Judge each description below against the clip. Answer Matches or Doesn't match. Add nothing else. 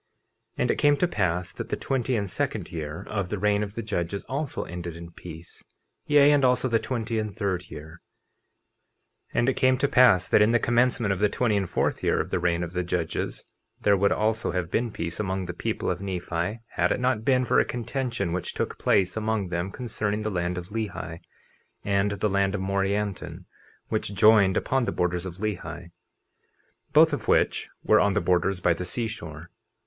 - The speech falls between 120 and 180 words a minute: Doesn't match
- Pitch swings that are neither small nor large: Matches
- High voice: Doesn't match